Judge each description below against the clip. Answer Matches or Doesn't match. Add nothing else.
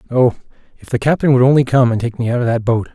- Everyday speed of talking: Doesn't match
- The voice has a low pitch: Matches